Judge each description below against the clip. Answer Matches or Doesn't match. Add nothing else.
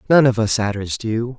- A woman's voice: Doesn't match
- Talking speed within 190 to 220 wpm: Matches